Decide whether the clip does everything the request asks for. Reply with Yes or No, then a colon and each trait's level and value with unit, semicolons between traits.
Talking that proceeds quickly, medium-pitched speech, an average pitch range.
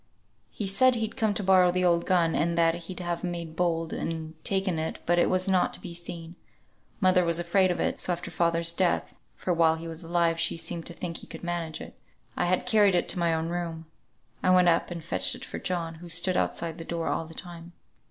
No: fast, 235 wpm; medium, 170 Hz; narrow, 1.6 semitones